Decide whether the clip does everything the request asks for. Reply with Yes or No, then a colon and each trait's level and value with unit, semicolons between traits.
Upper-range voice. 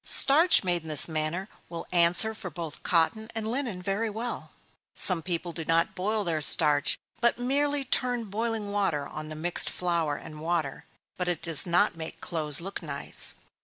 No: medium, 175 Hz